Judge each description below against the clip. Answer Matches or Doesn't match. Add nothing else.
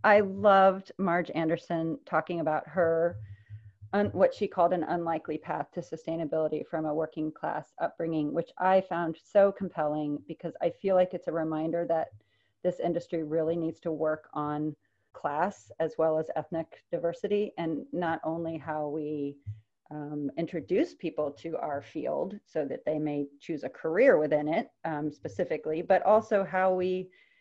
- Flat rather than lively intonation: Matches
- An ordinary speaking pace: Matches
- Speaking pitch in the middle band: Matches